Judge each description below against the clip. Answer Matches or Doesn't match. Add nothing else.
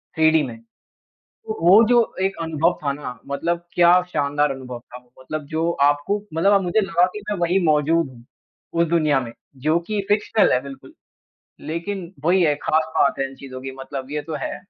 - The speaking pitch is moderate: Matches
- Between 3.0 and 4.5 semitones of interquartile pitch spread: Matches